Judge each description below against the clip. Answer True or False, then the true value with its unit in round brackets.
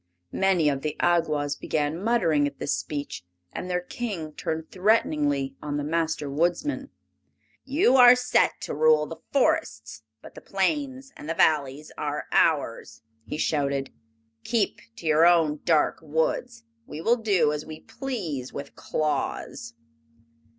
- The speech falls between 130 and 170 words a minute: True (145 wpm)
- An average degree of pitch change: False (7.2 semitones)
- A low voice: False (160 Hz)